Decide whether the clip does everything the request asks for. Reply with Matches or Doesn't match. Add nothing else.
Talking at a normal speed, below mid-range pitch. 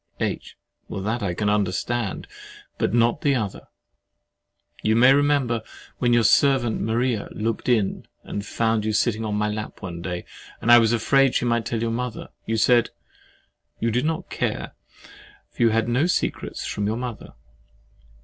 Matches